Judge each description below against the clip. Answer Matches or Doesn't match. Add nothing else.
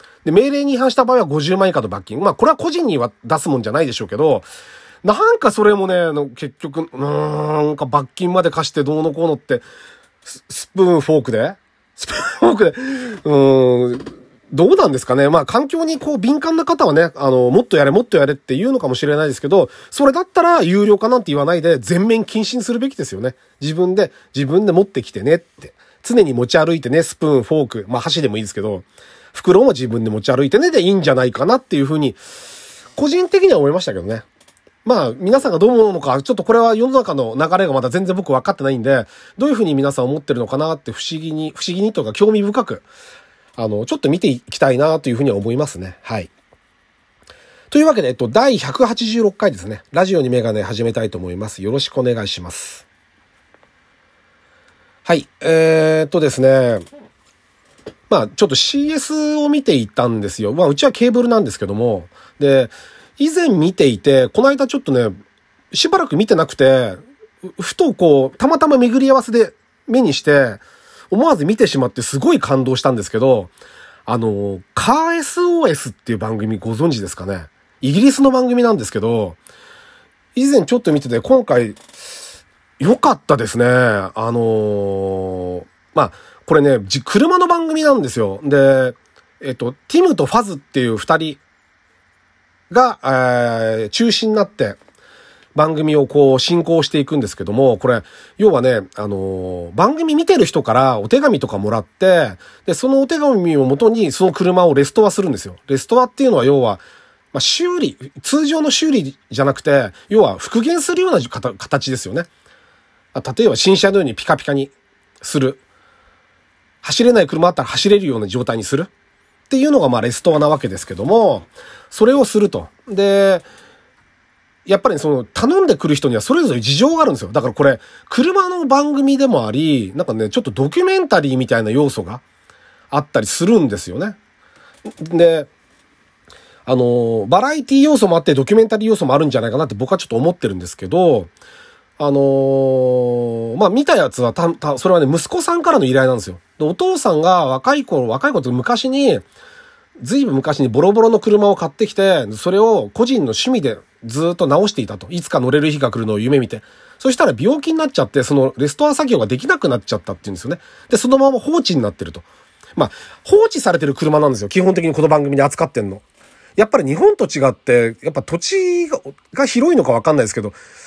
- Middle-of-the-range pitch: Matches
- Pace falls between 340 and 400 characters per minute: Matches